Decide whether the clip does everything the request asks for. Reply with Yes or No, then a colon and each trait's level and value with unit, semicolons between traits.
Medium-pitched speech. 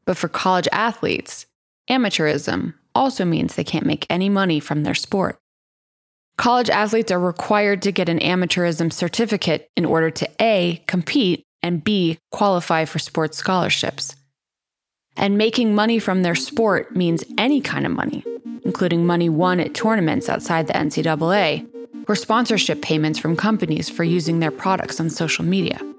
Yes: medium, 180 Hz